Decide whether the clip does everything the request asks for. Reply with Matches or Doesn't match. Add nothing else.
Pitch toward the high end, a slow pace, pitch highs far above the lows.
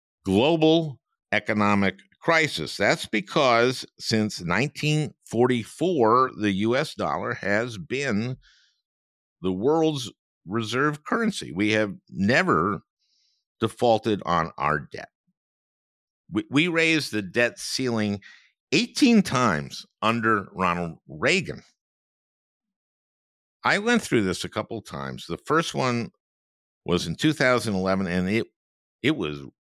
Doesn't match